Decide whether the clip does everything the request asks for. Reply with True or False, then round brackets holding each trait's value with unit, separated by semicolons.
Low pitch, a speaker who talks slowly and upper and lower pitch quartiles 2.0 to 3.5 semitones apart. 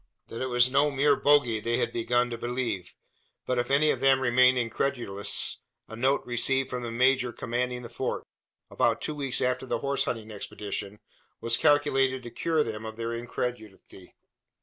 False (125 Hz; 175 wpm; 2.4 semitones)